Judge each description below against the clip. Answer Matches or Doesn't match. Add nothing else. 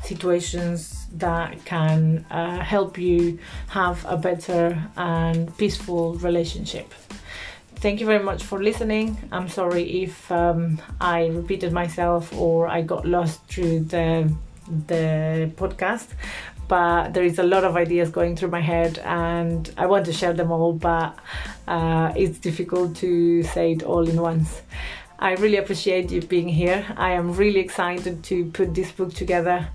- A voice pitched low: Doesn't match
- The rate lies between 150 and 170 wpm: Matches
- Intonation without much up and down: Matches